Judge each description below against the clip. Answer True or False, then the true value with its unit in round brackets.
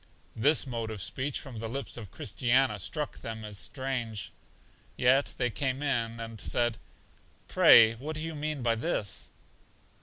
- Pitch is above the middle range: False (120 Hz)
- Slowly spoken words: False (155 wpm)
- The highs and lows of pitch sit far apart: False (3.5 semitones)